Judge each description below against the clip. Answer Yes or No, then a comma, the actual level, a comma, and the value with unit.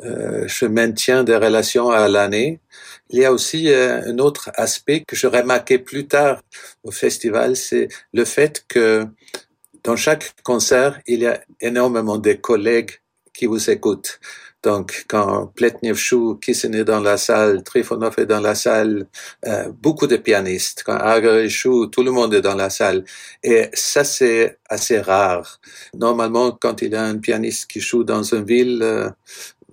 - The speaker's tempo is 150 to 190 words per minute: Yes, average, 170 wpm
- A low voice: Yes, low, 115 Hz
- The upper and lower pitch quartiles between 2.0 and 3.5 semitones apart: Yes, narrow, 2.6 semitones